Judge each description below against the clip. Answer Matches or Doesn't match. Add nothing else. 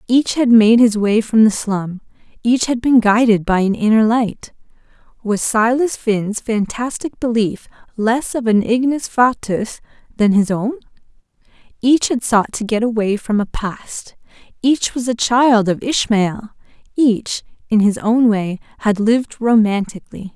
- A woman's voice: Matches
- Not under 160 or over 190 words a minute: Doesn't match